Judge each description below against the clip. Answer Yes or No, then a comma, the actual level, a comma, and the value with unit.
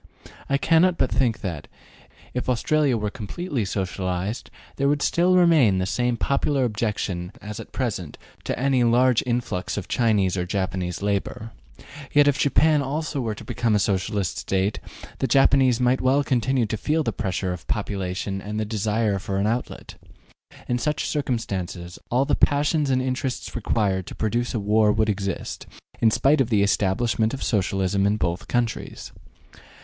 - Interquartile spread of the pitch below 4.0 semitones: No, average, 5.1 semitones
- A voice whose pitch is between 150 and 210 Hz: No, low, 110 Hz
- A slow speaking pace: No, average, 165 wpm